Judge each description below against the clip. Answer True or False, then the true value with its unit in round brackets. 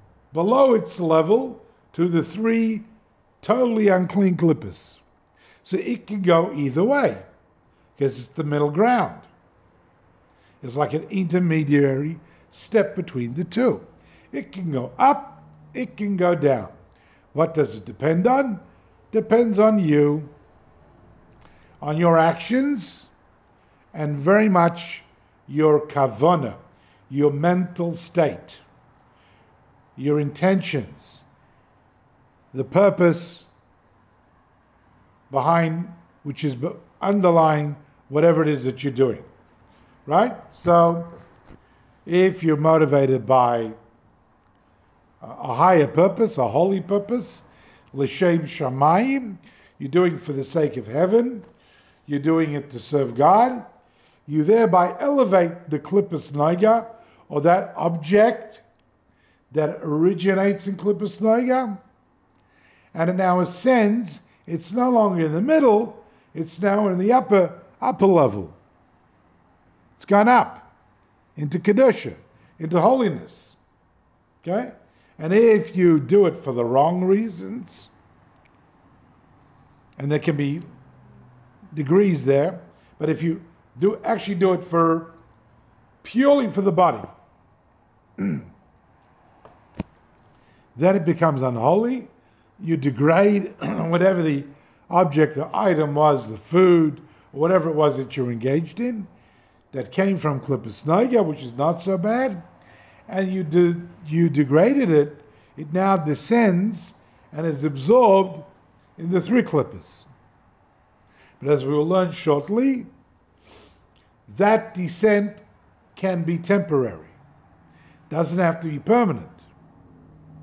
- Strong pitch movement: True (6.2 semitones)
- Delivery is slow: True (115 wpm)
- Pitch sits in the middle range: True (165 Hz)